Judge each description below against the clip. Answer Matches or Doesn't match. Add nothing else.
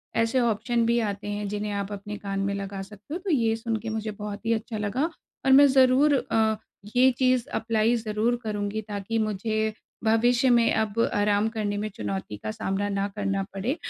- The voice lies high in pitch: Matches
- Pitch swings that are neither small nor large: Doesn't match